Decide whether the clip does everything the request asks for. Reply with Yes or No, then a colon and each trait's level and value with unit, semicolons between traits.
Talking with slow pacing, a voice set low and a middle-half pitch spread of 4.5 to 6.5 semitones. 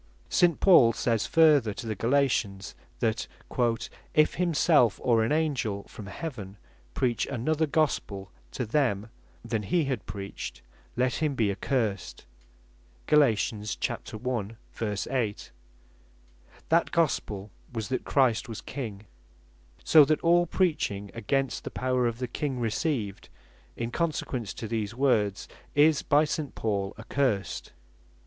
Yes: slow, 125 wpm; low, 120 Hz; wide, 5.6 semitones